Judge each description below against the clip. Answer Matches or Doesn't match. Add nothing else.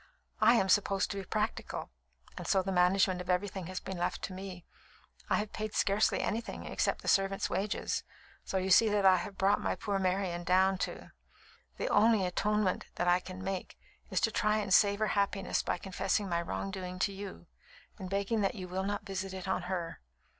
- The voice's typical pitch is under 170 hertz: Doesn't match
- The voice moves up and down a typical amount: Doesn't match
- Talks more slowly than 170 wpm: Doesn't match